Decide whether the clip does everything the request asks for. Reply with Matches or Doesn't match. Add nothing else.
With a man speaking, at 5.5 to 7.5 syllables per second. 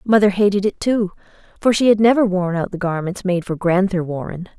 Doesn't match